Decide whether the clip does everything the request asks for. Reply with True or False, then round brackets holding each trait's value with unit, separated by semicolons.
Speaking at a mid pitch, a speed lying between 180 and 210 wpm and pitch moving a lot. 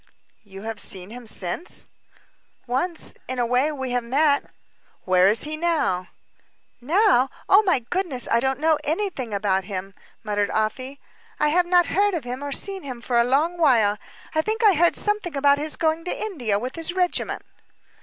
False (275 Hz; 185 wpm; 6.7 semitones)